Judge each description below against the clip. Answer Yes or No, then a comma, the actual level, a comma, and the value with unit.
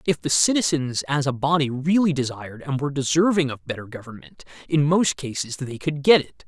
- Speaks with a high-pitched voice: No, medium, 140 Hz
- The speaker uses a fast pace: No, average, 195 wpm